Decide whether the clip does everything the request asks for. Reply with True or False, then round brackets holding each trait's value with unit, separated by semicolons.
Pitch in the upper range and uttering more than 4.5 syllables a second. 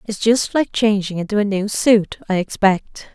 False (205 Hz; 4.4 syllables/s)